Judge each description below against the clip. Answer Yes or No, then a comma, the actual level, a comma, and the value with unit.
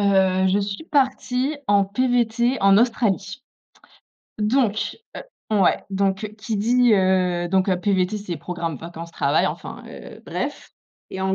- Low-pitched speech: No, high, 200 Hz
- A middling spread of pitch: Yes, average, 3.6 semitones